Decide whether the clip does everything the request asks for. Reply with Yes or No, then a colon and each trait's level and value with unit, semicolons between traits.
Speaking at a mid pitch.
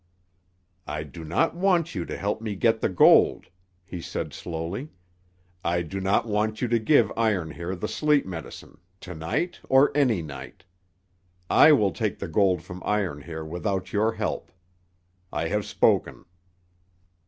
No: low, 100 Hz